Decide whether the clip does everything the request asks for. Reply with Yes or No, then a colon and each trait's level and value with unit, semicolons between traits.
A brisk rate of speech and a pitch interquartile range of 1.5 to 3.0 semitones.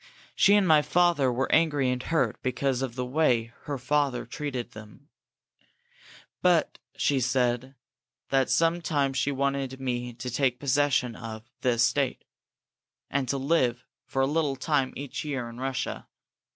No: average, 150 wpm; narrow, 2.5 semitones